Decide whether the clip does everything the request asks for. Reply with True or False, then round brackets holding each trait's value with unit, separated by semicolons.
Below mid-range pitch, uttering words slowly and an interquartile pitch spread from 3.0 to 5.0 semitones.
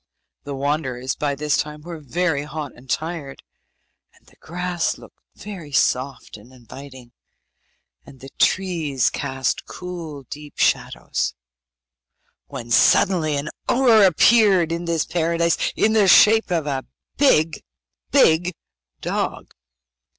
False (155 Hz; 120 wpm; 4.4 semitones)